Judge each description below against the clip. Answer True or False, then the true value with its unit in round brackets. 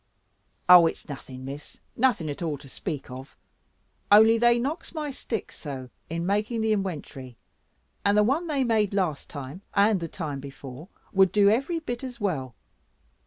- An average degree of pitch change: False (7.9 semitones)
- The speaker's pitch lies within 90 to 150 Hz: False (195 Hz)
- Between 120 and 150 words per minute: False (165 wpm)